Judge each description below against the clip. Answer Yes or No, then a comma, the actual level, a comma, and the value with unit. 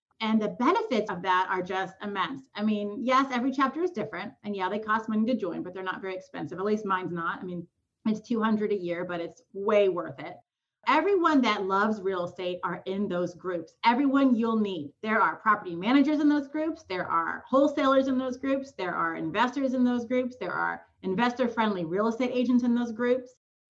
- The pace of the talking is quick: Yes, fast, 210 wpm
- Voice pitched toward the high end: Yes, high, 215 Hz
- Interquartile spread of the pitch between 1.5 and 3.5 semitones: No, average, 5.3 semitones